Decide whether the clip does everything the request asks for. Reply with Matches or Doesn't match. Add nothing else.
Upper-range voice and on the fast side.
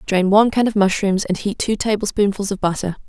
Matches